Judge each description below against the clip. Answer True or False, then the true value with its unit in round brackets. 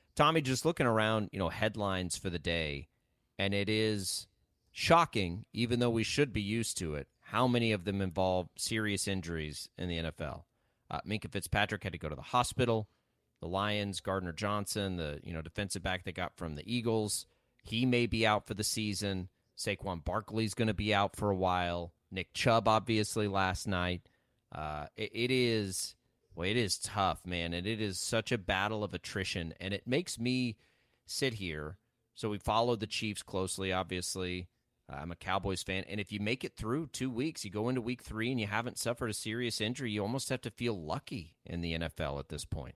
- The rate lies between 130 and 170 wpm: False (200 wpm)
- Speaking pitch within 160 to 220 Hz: False (100 Hz)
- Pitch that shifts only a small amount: False (4.1 semitones)